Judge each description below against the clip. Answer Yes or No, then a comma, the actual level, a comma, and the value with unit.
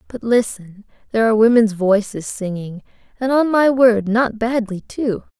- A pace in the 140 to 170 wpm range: Yes, average, 155 wpm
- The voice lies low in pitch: No, high, 225 Hz